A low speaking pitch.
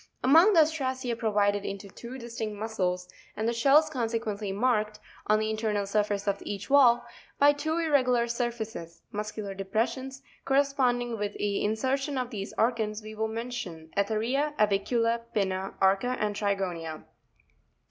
No: high, 220 Hz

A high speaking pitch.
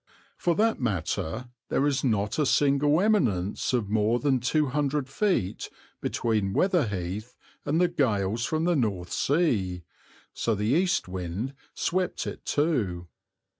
No: low, 125 Hz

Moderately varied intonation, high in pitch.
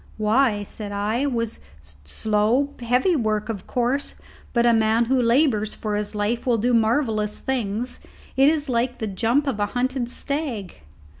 Yes: average, 3.4 semitones; high, 230 Hz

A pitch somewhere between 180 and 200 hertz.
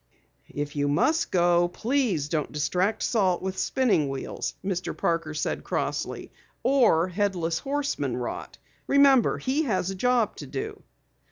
Yes: high, 190 Hz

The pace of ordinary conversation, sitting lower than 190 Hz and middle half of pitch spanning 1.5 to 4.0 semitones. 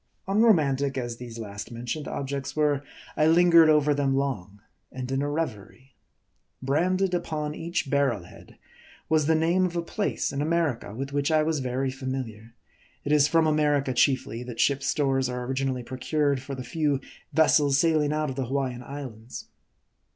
Yes: average, 170 wpm; medium, 140 Hz; average, 3.1 semitones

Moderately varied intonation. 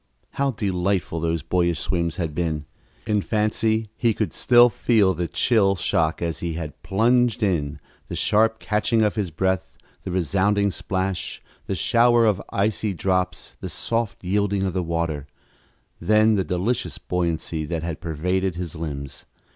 Yes: average, 4.2 semitones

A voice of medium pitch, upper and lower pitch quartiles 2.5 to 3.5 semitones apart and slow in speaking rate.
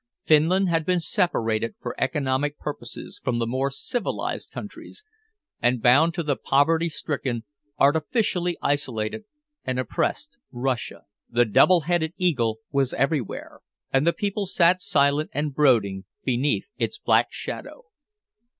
No: medium, 145 Hz; average, 5.3 semitones; slow, 130 wpm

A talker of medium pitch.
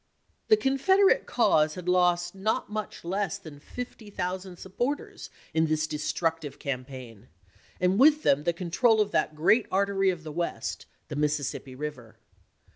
Yes: medium, 175 Hz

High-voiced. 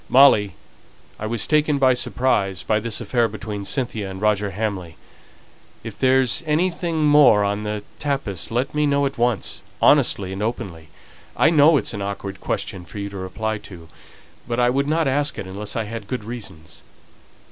No: low, 110 Hz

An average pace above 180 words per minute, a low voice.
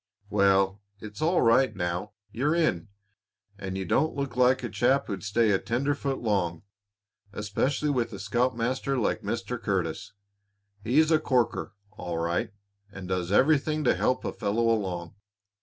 No: average, 150 wpm; low, 115 Hz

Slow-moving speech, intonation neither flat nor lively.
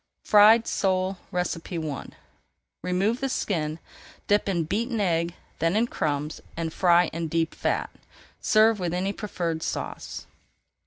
Yes: slow, 125 wpm; average, 3.8 semitones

